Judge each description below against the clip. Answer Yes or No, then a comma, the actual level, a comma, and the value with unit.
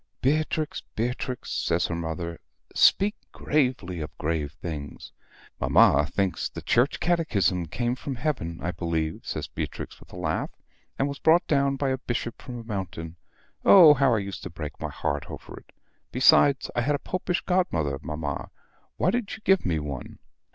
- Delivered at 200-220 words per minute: No, average, 170 wpm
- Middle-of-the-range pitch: No, low, 115 Hz